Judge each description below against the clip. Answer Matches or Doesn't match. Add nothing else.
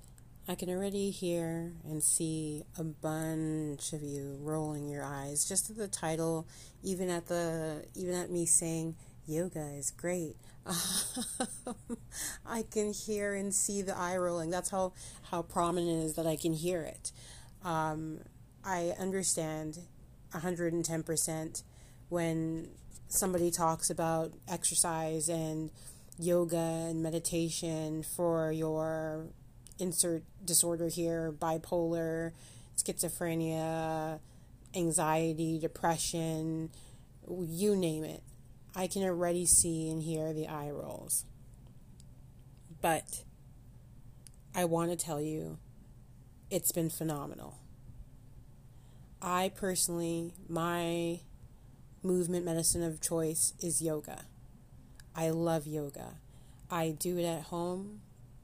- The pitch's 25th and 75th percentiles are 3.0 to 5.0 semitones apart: Doesn't match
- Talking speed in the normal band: Doesn't match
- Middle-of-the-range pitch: Matches